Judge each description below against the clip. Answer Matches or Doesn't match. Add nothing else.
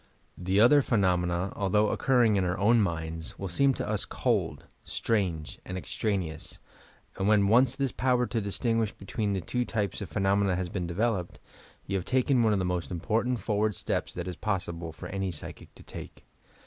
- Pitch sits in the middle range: Doesn't match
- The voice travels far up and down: Doesn't match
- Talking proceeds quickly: Doesn't match